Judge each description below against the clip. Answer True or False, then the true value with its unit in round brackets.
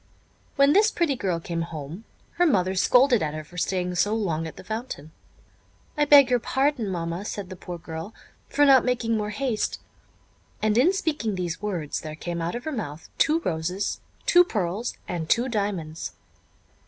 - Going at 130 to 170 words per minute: False (180 wpm)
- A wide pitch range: True (7.0 semitones)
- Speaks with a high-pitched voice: True (205 Hz)